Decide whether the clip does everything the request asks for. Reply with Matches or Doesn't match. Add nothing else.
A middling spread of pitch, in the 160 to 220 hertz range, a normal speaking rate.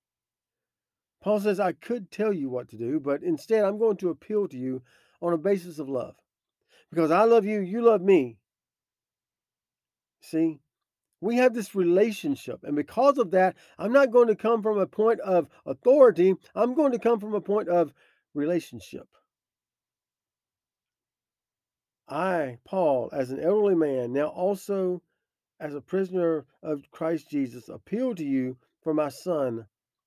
Doesn't match